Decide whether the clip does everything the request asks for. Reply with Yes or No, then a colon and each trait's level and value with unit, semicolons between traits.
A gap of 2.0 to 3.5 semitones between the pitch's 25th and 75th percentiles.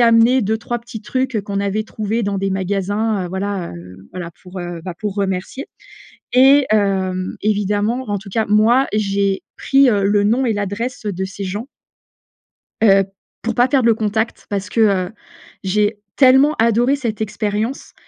Yes: average, 2.8 semitones